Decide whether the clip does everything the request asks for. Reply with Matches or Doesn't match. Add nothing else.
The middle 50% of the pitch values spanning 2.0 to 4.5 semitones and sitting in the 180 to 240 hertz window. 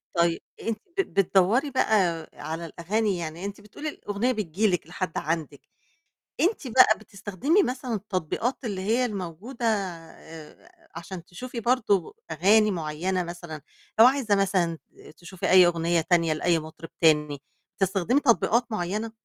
Doesn't match